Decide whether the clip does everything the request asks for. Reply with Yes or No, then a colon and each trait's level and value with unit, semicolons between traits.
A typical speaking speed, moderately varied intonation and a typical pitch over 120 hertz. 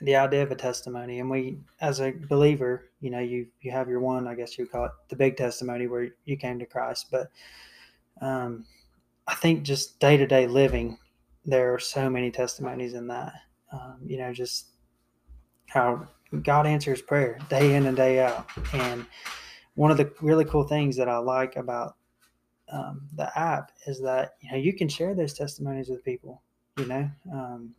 No: average, 190 wpm; narrow, 2.3 semitones; low, 130 Hz